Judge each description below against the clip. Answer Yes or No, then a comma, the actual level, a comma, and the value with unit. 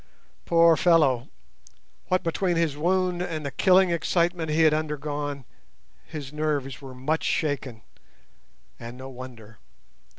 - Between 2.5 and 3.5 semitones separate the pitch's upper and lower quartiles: No, average, 3.9 semitones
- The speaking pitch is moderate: Yes, medium, 150 Hz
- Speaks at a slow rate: Yes, slow, 125 wpm